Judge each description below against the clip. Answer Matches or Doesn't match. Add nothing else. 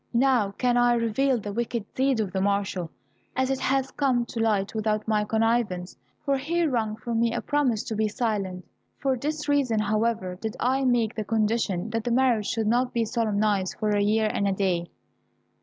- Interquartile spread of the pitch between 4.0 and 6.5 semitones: Doesn't match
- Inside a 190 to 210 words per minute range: Matches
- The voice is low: Doesn't match